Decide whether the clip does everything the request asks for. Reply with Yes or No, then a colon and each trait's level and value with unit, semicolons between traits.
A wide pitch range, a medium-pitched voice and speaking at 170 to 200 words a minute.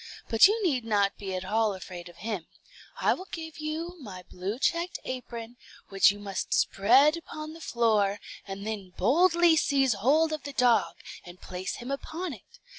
No: wide, 7.8 semitones; high, 240 Hz; average, 180 wpm